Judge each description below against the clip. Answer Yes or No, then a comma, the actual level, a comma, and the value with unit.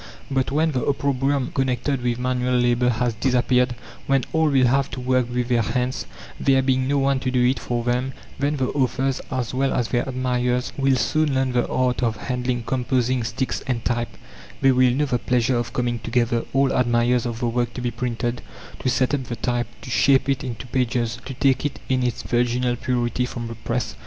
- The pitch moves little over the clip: Yes, narrow, 1.5 semitones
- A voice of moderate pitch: No, low, 125 Hz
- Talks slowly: No, fast, 205 wpm